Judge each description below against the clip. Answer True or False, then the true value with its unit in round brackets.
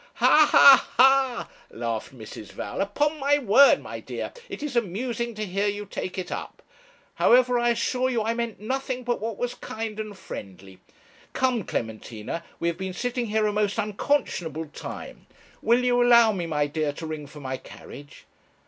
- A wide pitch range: True (6.7 semitones)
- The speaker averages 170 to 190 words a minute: True (175 wpm)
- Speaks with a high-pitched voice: True (215 Hz)